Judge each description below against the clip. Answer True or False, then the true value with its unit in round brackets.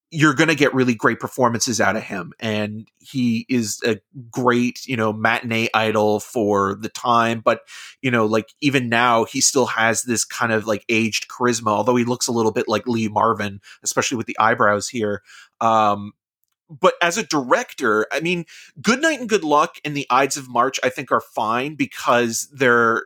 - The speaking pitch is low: True (120 Hz)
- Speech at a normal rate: True (195 wpm)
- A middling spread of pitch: True (3.6 semitones)